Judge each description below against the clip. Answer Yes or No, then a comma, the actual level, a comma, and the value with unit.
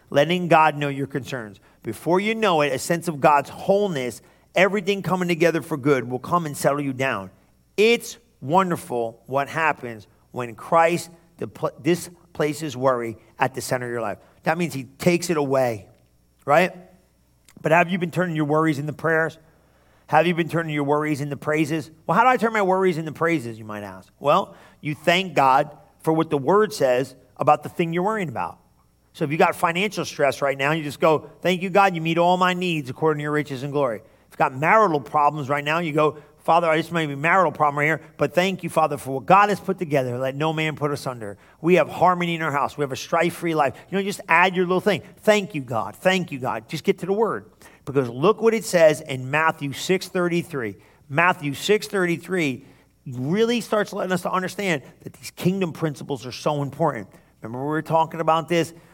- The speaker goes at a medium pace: No, fast, 210 wpm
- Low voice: No, medium, 155 Hz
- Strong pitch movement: No, average, 4.4 semitones